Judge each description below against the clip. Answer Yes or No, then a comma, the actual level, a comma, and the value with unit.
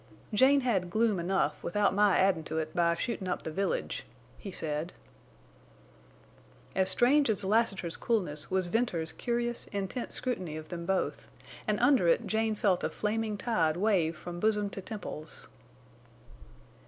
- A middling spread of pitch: Yes, average, 4.4 semitones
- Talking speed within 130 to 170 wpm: Yes, average, 150 wpm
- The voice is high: Yes, high, 195 Hz